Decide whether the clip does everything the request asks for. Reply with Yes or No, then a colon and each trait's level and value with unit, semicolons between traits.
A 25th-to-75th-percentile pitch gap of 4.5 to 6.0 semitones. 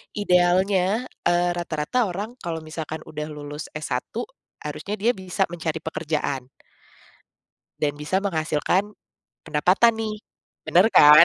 No: average, 4.0 semitones